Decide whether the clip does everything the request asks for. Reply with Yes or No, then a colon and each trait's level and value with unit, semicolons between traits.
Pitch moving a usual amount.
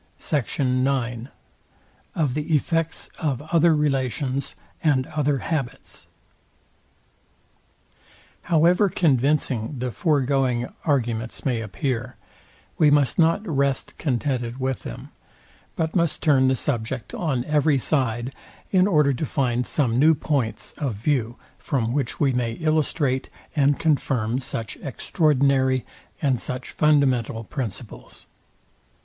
Yes: average, 3.4 semitones